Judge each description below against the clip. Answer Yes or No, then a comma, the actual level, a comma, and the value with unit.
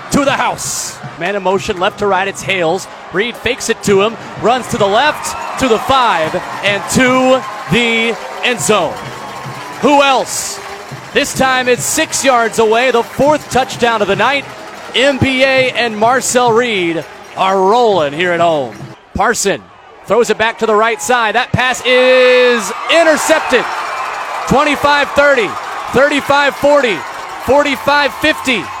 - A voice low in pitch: No, high, 245 Hz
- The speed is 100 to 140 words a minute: Yes, slow, 135 wpm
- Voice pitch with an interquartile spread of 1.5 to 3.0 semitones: No, average, 4.0 semitones